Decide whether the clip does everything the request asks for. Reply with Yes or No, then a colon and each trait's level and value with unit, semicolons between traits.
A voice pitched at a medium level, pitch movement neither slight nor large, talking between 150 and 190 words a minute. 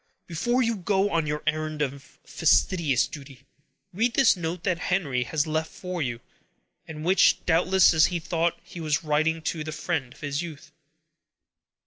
Yes: medium, 160 Hz; average, 3.0 semitones; average, 160 wpm